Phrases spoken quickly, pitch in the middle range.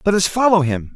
Yes: fast, 250 wpm; medium, 175 Hz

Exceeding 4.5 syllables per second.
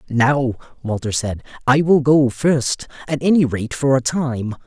No: 4.4 syllables/s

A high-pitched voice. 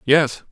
No: medium, 140 Hz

